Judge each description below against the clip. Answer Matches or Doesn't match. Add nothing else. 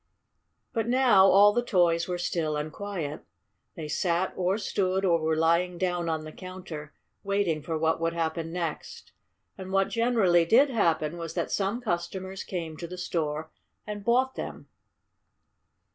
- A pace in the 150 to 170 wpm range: Matches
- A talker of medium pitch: Matches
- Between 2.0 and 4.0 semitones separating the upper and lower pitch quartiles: Matches